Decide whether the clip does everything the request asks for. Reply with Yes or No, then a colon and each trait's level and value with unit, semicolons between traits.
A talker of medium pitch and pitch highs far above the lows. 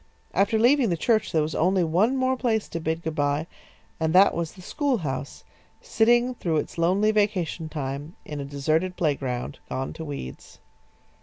Yes: medium, 170 Hz; wide, 6.2 semitones